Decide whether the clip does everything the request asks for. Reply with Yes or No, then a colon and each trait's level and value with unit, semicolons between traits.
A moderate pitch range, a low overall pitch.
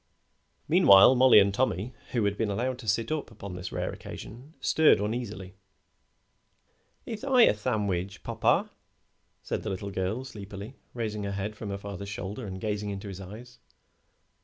Yes: average, 3.6 semitones; low, 105 Hz